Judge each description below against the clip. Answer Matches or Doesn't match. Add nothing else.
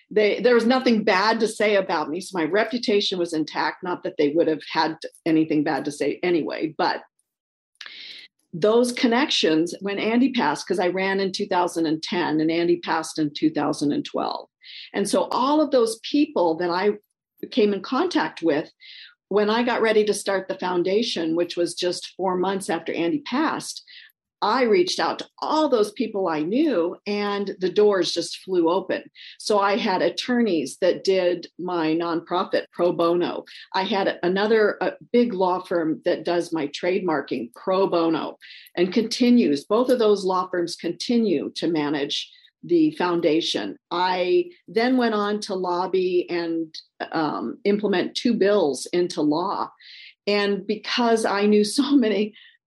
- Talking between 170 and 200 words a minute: Doesn't match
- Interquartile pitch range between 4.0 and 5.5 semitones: Matches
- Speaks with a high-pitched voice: Matches